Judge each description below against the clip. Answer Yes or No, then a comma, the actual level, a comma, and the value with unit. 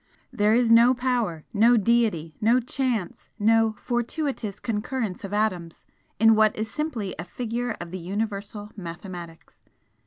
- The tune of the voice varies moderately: Yes, average, 3.5 semitones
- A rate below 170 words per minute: Yes, slow, 135 wpm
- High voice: Yes, high, 220 Hz